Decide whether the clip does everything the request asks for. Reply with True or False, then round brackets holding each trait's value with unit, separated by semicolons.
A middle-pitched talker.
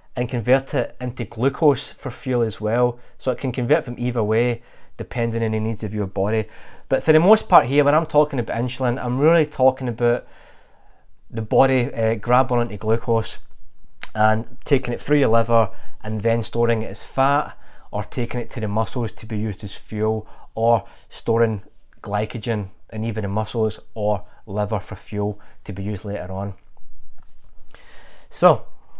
False (115 Hz)